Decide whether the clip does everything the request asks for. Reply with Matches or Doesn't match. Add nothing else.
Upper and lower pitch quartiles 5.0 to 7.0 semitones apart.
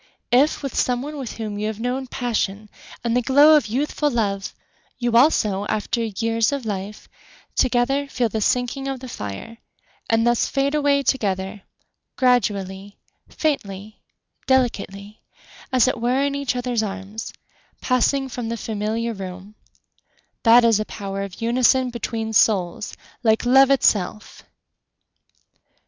Doesn't match